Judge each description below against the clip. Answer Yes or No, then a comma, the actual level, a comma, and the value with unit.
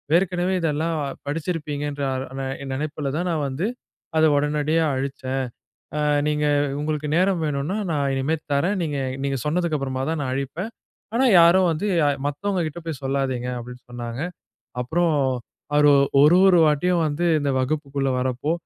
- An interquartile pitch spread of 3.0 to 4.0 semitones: Yes, average, 3.4 semitones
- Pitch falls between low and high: Yes, medium, 150 Hz